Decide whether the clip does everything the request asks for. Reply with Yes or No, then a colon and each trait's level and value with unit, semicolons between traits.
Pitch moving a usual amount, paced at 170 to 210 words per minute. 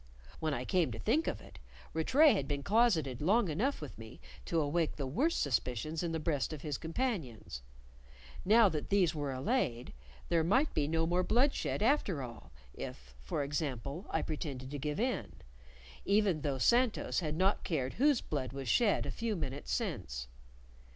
No: wide, 7.1 semitones; average, 175 wpm